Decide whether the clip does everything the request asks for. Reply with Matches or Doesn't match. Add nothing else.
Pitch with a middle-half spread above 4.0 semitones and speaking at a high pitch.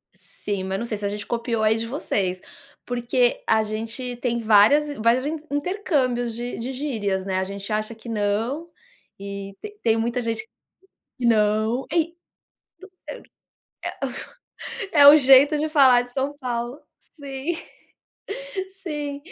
Matches